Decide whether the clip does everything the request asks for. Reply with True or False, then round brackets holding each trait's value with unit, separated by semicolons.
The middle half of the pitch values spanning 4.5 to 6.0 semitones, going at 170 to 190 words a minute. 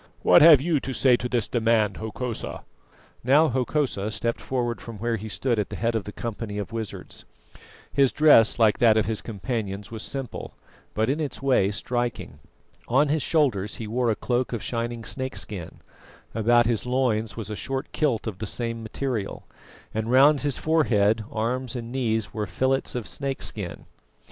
False (3.2 semitones; 175 wpm)